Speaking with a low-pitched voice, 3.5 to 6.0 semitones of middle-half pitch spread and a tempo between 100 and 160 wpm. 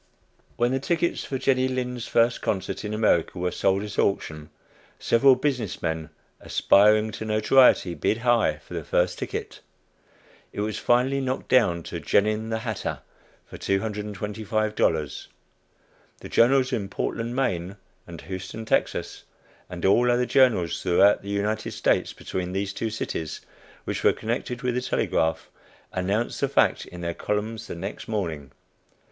Yes: low, 110 Hz; average, 4.4 semitones; average, 150 wpm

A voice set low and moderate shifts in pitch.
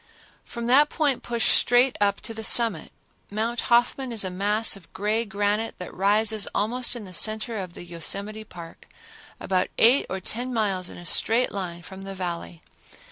No: high, 210 Hz; average, 3.7 semitones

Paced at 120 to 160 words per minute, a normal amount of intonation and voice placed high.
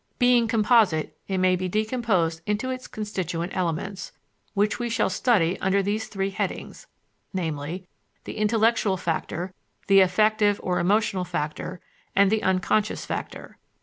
Yes: slow, 135 wpm; average, 3.1 semitones; high, 195 Hz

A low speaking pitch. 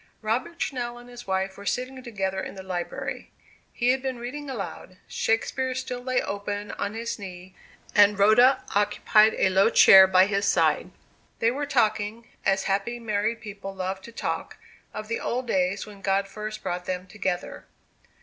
No: high, 210 Hz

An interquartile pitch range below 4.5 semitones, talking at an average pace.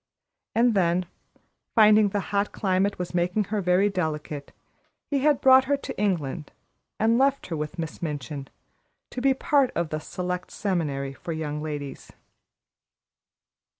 No: wide, 5.6 semitones; average, 145 wpm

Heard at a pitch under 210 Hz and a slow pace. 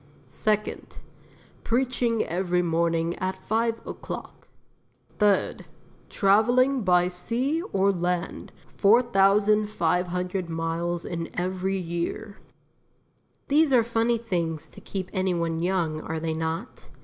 Yes: medium, 185 Hz; slow, 105 wpm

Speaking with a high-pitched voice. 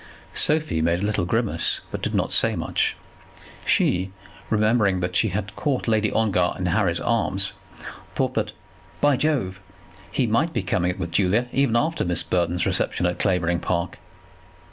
No: very low, 95 Hz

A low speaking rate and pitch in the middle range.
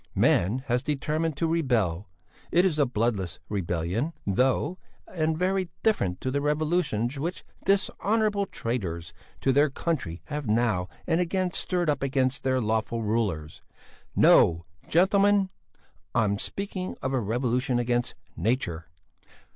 No: slow, 130 wpm; low, 130 Hz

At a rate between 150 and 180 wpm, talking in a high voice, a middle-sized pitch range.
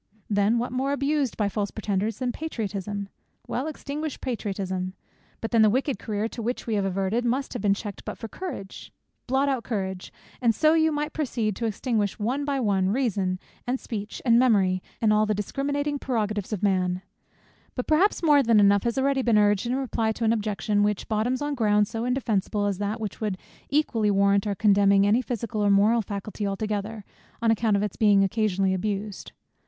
No: average, 190 wpm; high, 215 Hz; average, 3.7 semitones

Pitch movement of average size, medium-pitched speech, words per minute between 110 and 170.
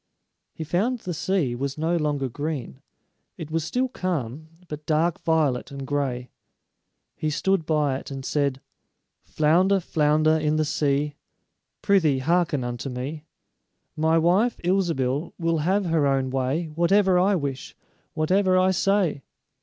Yes: average, 4.1 semitones; medium, 155 Hz; average, 140 wpm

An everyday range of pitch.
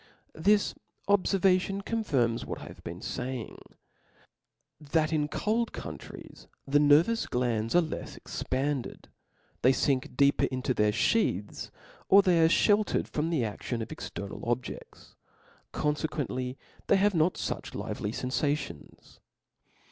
No: wide, 6.6 semitones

